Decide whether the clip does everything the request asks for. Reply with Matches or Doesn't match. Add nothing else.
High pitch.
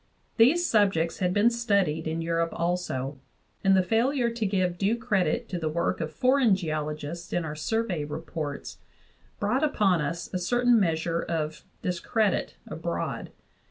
Doesn't match